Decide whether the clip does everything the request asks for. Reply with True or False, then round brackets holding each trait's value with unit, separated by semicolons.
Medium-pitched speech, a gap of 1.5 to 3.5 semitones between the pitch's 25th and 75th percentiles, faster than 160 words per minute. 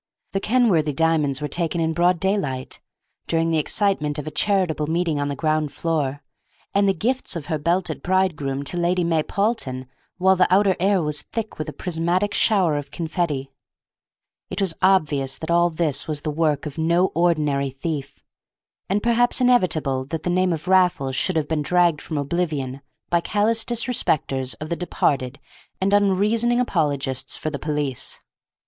False (165 Hz; 4.3 semitones; 170 wpm)